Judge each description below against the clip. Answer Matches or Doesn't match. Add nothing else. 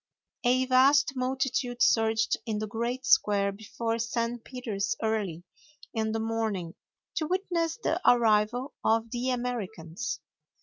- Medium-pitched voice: Doesn't match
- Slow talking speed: Matches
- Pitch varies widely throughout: Doesn't match